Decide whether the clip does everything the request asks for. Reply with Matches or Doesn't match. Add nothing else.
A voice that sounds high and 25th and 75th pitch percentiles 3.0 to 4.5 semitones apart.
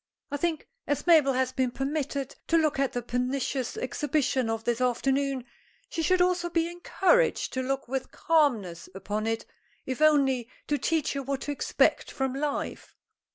Matches